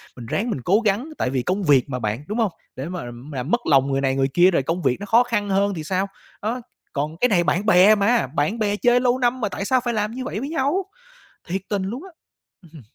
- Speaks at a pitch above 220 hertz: No, high, 200 Hz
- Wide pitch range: Yes, wide, 7.8 semitones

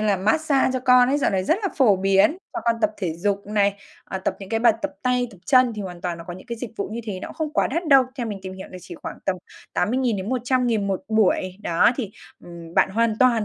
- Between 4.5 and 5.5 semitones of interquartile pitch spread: Yes, average, 4.8 semitones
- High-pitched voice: Yes, high, 215 Hz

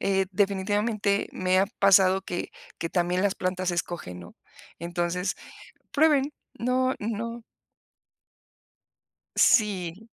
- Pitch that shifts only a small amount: No, average, 3.0 semitones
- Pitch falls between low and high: No, high, 195 Hz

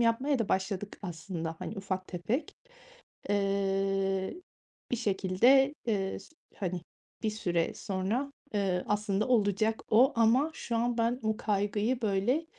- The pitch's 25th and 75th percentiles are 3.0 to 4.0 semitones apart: Yes, average, 3.3 semitones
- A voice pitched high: Yes, high, 205 Hz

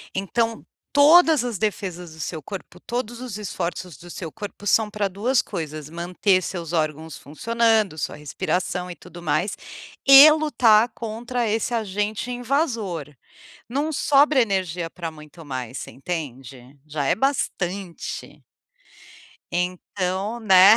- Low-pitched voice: No, high, 195 Hz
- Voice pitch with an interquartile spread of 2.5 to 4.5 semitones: No, wide, 5.6 semitones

